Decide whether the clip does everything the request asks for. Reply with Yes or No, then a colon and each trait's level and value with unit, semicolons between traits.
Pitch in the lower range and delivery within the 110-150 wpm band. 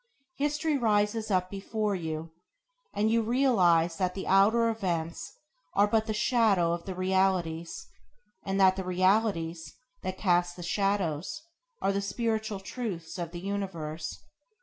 No: high, 195 Hz; average, 140 wpm